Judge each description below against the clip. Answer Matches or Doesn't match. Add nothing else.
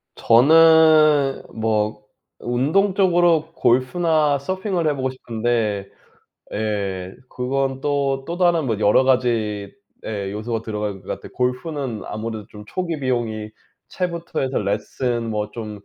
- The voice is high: Doesn't match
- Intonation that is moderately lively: Doesn't match